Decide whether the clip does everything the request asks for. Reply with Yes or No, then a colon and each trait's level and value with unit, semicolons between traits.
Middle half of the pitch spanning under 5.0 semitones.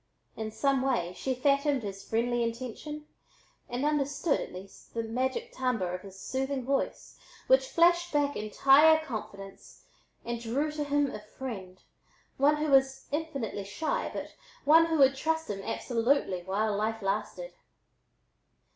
No: average, 5.3 semitones